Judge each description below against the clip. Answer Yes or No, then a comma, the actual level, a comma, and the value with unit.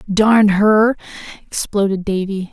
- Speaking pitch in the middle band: No, high, 205 Hz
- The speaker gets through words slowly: Yes, slow, 95 wpm